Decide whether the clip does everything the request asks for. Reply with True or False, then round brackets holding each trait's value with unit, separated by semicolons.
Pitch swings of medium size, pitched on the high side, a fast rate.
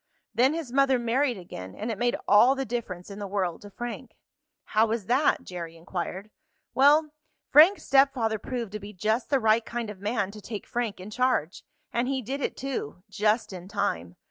False (4.5 semitones; 225 Hz; 195 wpm)